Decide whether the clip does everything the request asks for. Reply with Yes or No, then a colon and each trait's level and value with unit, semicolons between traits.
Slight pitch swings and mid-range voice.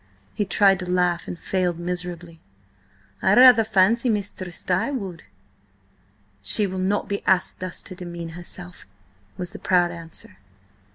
Yes: narrow, 2.1 semitones; medium, 180 Hz